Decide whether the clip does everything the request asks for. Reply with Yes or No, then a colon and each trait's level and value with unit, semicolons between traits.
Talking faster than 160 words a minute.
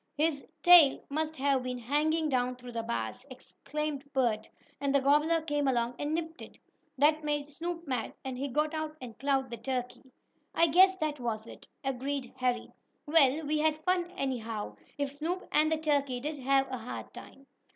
Yes: average, 180 wpm